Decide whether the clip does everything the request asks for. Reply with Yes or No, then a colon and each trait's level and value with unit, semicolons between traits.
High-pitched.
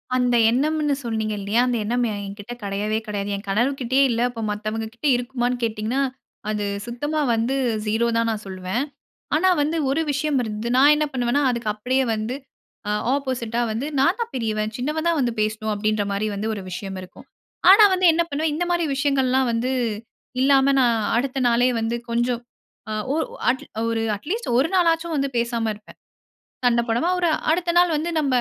Yes: high, 240 Hz